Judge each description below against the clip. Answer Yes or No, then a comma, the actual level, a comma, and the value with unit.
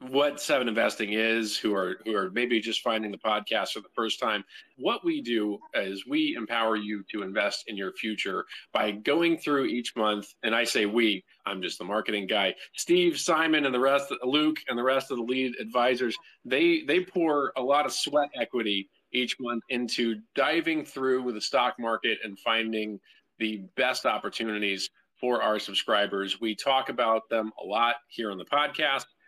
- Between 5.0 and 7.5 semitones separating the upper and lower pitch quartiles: No, average, 4.5 semitones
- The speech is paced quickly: No, average, 185 wpm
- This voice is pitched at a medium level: No, low, 120 Hz